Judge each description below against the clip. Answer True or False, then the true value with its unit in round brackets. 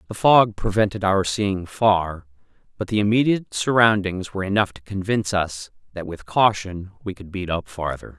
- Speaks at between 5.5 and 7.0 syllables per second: False (5.0 syllables/s)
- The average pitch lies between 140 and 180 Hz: False (100 Hz)